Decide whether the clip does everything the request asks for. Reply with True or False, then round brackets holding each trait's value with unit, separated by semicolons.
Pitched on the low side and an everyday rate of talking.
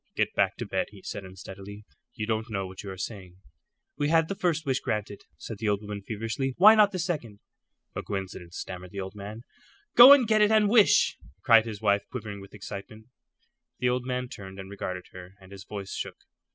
False (105 Hz; 210 wpm)